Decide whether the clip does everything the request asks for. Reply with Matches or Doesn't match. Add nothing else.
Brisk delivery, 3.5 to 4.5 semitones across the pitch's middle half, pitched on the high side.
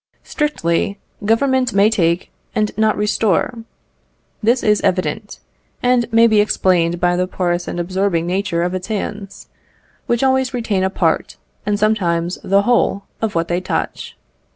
Doesn't match